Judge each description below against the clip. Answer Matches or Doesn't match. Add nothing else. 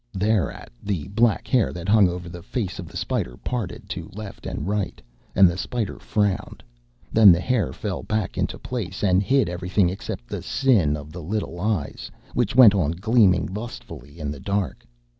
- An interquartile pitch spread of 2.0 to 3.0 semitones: Doesn't match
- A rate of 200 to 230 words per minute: Doesn't match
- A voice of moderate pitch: Doesn't match